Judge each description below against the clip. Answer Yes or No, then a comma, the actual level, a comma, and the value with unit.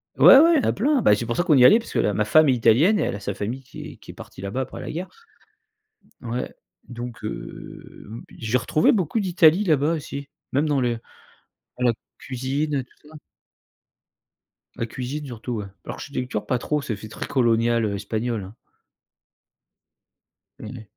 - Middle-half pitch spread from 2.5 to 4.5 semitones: No, average, 5.0 semitones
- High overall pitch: No, low, 125 Hz